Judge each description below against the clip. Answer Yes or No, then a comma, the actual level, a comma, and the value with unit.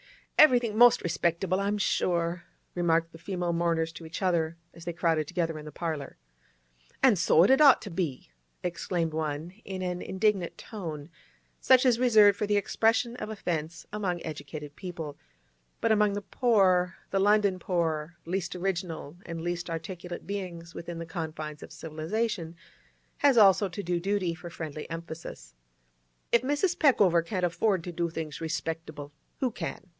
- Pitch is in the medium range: Yes, medium, 175 Hz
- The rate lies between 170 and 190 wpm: No, average, 160 wpm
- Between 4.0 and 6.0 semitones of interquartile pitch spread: No, average, 3.6 semitones